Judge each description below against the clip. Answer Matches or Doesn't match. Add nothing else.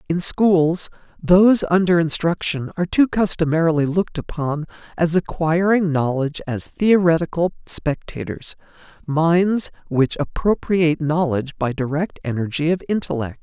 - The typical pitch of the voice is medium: Matches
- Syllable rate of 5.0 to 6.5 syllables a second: Doesn't match